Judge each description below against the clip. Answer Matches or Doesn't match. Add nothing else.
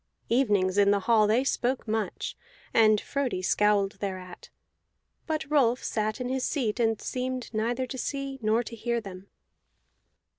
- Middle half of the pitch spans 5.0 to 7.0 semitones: Doesn't match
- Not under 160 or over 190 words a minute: Doesn't match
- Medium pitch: Doesn't match